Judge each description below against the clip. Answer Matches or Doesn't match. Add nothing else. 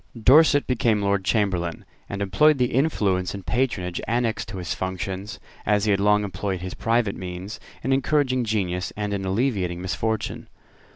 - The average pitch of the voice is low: Matches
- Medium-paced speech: Matches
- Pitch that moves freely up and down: Doesn't match